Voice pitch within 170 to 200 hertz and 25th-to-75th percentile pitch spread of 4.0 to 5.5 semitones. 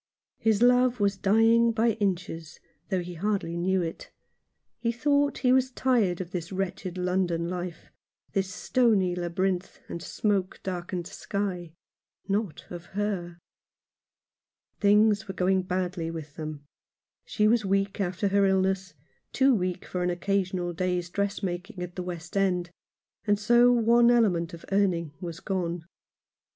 No: high, 190 Hz; average, 3.0 semitones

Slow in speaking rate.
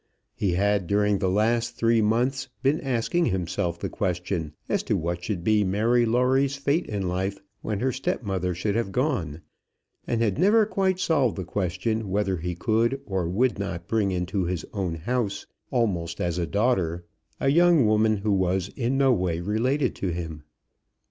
No: average, 175 wpm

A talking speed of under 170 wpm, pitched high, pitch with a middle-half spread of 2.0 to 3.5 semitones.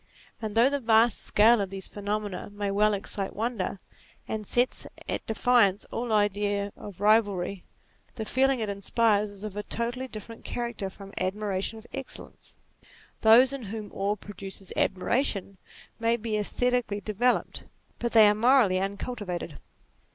Yes: average, 150 wpm; high, 210 Hz; average, 2.7 semitones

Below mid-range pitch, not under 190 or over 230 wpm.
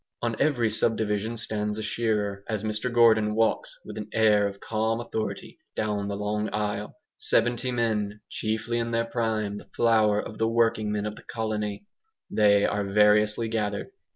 No: low, 110 Hz; average, 165 wpm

